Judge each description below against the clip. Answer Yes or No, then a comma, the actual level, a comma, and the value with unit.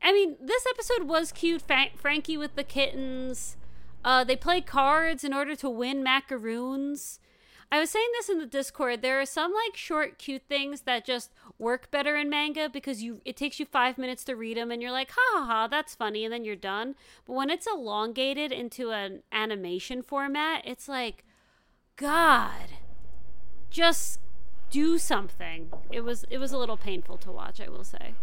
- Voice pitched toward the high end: Yes, very high, 270 Hz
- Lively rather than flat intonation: No, average, 4.4 semitones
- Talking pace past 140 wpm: Yes, average, 180 wpm